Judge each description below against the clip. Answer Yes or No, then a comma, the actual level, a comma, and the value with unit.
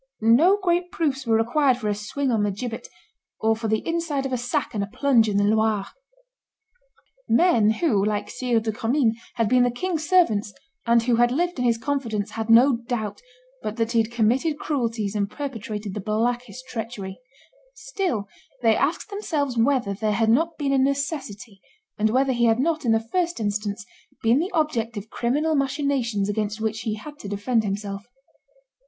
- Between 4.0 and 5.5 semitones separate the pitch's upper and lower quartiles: Yes, average, 4.5 semitones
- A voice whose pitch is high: Yes, high, 235 Hz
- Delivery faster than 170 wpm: Yes, average, 185 wpm